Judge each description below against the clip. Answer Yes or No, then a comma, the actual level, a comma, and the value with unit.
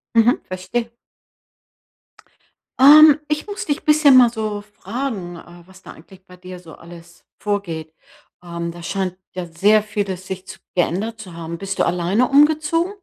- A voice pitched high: Yes, high, 195 Hz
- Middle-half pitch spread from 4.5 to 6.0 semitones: Yes, wide, 5.6 semitones